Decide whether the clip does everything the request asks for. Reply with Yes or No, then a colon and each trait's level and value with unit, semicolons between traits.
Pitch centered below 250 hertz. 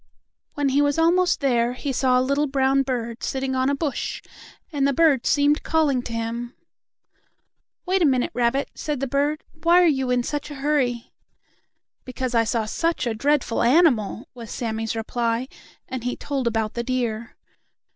No: very high, 260 Hz